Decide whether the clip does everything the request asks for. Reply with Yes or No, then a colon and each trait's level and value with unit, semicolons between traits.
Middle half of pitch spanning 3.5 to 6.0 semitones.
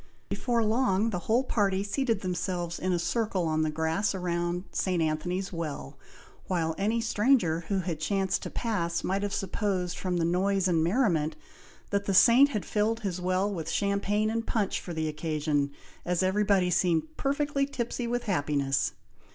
Yes: average, 3.9 semitones